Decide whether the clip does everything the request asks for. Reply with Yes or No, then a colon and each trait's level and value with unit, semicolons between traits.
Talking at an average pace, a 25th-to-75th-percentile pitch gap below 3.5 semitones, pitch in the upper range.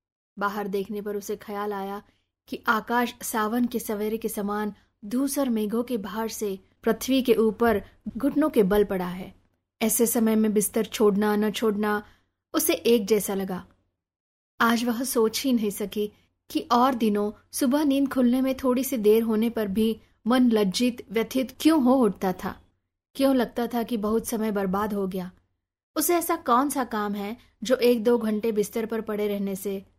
Yes: average, 170 wpm; average, 2.8 semitones; high, 220 Hz